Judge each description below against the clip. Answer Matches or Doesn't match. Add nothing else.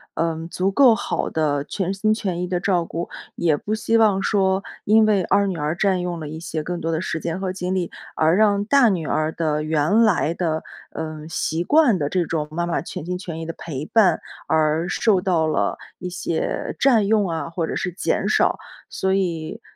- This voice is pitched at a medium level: Matches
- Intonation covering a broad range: Doesn't match